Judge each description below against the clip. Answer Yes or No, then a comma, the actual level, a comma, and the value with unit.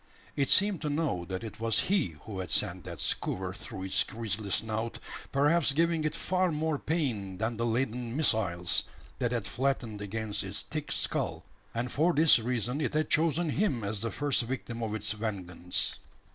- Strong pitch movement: Yes, wide, 6.3 semitones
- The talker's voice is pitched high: No, low, 115 Hz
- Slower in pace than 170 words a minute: No, average, 180 wpm